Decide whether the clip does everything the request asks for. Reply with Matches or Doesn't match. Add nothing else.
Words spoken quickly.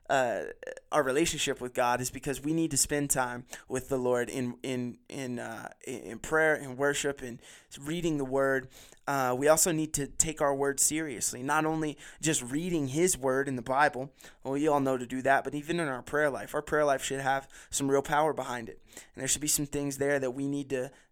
Matches